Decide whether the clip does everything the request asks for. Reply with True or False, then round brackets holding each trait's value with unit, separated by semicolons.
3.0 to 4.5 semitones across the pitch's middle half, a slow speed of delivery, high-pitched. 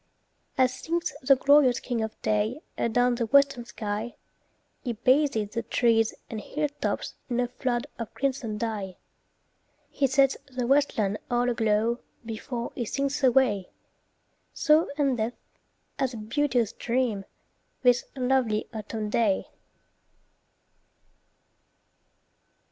True (3.3 semitones; 115 wpm; 240 Hz)